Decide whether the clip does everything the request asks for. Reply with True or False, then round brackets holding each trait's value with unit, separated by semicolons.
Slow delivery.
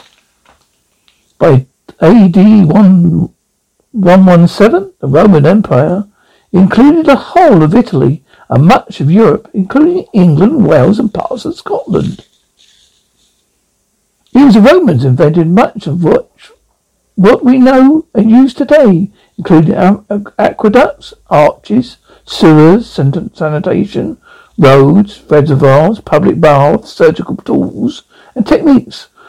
True (100 wpm)